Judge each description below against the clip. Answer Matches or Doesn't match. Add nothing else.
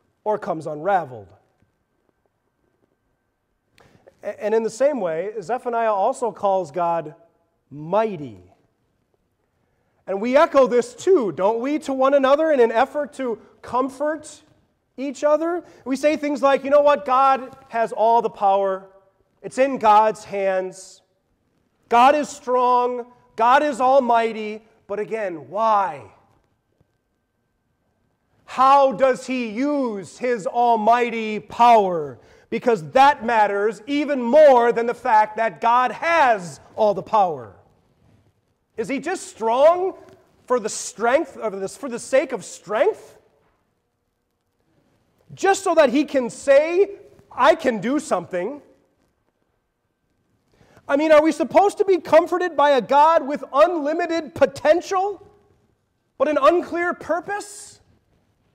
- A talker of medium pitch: Doesn't match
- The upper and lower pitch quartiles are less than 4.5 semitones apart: Doesn't match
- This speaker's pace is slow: Matches